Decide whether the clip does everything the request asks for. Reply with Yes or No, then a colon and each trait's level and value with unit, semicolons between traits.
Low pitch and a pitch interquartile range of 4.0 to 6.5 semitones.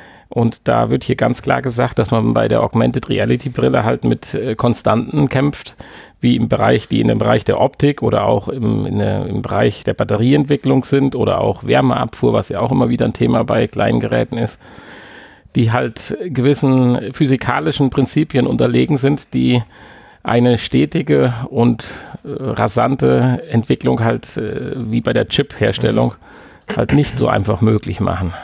Yes: low, 120 Hz; average, 4.8 semitones